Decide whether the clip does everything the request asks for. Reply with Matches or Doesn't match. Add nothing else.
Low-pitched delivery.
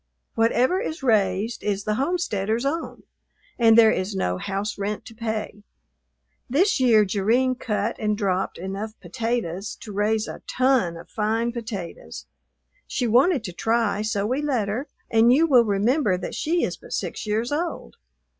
Doesn't match